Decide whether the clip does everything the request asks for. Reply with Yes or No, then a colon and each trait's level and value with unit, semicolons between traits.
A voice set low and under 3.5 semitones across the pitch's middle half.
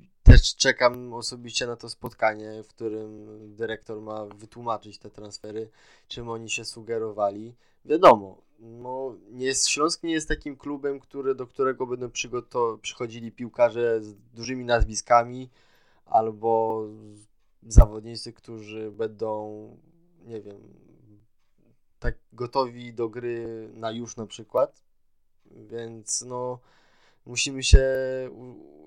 Yes: low, 115 Hz; narrow, 2.4 semitones